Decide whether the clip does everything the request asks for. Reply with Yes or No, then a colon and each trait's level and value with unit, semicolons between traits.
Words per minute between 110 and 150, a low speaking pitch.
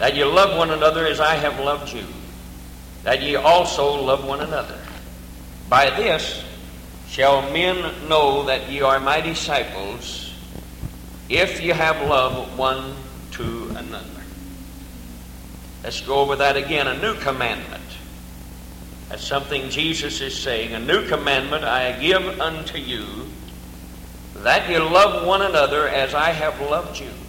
Yes: average, 140 wpm; low, 130 Hz